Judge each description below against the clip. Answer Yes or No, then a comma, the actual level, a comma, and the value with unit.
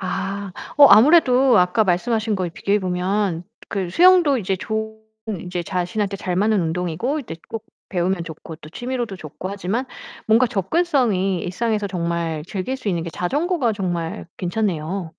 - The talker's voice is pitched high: Yes, high, 195 Hz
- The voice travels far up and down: No, average, 4.2 semitones